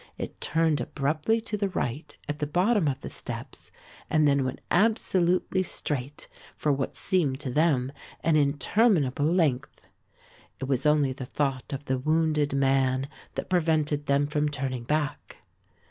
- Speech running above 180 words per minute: No, average, 150 wpm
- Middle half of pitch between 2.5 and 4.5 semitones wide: Yes, average, 3.1 semitones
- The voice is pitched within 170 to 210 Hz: No, medium, 145 Hz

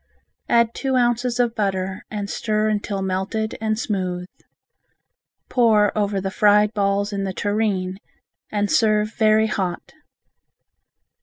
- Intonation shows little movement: Yes, narrow, 1.9 semitones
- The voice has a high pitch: Yes, high, 210 Hz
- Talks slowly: Yes, slow, 125 wpm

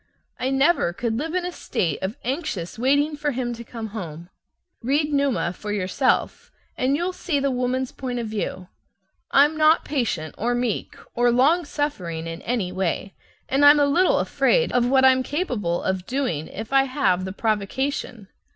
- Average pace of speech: Yes, average, 175 wpm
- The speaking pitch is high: Yes, very high, 250 Hz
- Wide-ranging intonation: Yes, wide, 6.0 semitones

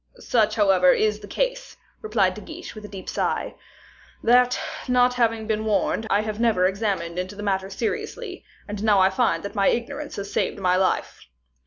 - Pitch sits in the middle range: No, high, 215 Hz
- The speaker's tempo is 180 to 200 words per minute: Yes, average, 185 wpm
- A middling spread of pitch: Yes, average, 3.4 semitones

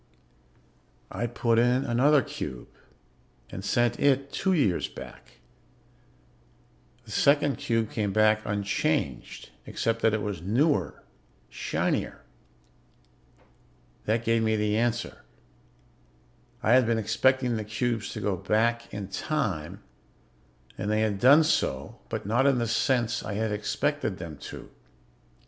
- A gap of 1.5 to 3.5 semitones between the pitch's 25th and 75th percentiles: Yes, average, 3.2 semitones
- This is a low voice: Yes, low, 115 Hz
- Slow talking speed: Yes, slow, 125 wpm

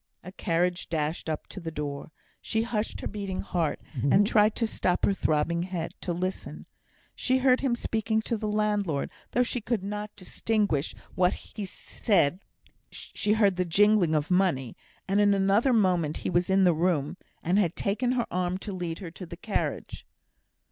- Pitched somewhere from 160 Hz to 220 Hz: Yes, high, 190 Hz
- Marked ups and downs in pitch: No, average, 3.7 semitones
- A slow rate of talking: No, average, 175 wpm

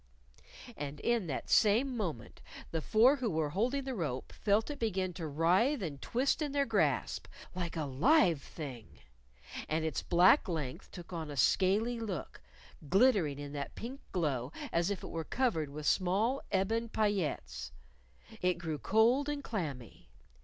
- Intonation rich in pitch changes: Yes, wide, 7.1 semitones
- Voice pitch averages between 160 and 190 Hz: Yes, medium, 185 Hz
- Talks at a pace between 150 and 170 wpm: Yes, average, 160 wpm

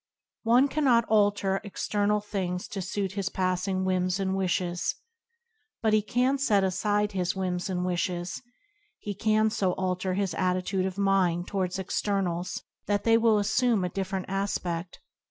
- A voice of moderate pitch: No, high, 195 Hz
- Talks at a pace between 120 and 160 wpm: Yes, average, 150 wpm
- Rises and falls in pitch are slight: Yes, narrow, 2.3 semitones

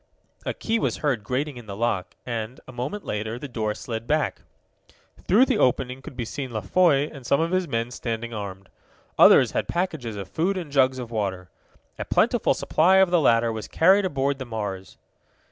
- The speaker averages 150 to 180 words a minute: No, average, 195 wpm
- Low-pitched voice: Yes, low, 125 Hz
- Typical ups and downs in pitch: No, wide, 5.7 semitones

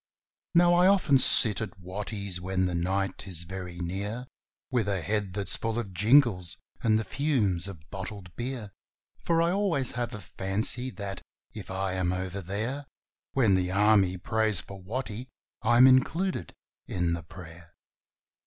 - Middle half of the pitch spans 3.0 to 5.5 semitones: Yes, average, 4.6 semitones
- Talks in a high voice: No, low, 100 Hz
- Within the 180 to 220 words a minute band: No, average, 155 wpm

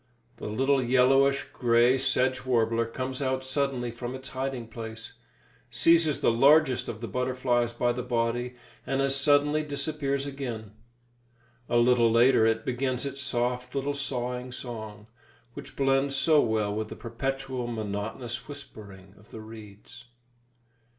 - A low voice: Yes, low, 125 Hz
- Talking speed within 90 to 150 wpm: Yes, average, 140 wpm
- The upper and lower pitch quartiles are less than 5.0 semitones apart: Yes, average, 2.7 semitones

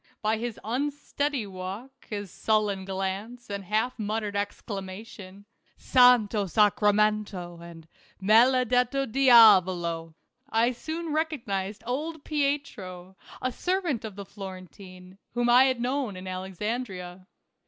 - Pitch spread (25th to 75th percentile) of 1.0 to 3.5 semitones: No, average, 4.7 semitones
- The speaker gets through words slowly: Yes, slow, 125 wpm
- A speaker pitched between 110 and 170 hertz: No, high, 215 Hz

